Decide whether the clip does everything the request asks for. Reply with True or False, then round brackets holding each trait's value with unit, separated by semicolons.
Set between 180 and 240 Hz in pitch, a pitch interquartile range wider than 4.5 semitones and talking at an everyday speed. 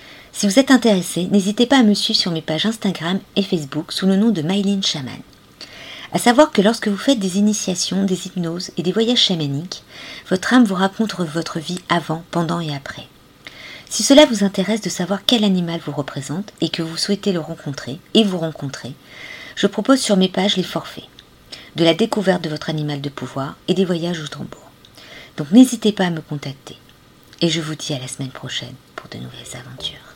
False (185 Hz; 4.2 semitones; 205 wpm)